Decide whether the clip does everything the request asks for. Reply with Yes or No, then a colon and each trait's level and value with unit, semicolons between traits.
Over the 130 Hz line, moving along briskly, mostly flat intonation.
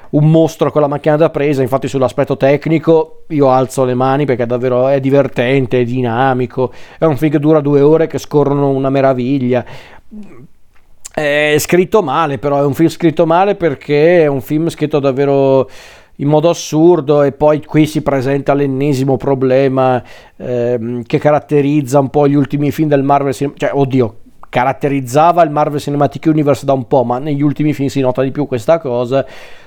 Yes: medium, 140 Hz; fast, 180 wpm; narrow, 2.3 semitones